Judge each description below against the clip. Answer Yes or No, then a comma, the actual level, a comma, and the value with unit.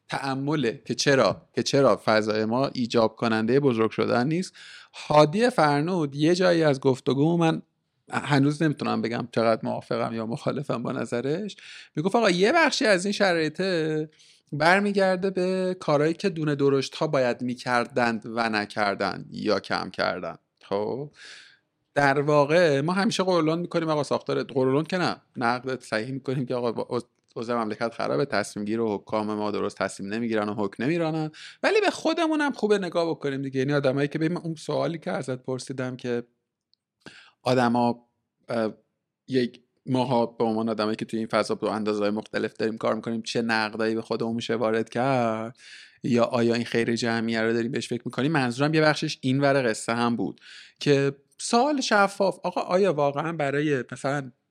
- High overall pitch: No, low, 130 Hz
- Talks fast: Yes, fast, 160 wpm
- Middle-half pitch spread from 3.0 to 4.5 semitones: No, average, 5.1 semitones